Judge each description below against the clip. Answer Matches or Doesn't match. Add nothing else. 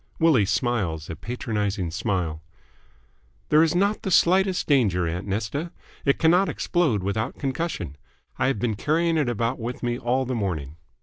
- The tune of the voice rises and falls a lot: Matches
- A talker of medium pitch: Doesn't match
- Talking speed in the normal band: Matches